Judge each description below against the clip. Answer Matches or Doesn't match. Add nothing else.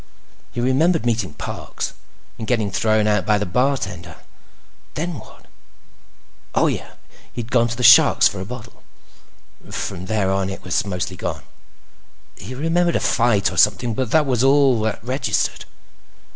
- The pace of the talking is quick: Doesn't match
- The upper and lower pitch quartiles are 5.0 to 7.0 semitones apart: Doesn't match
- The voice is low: Matches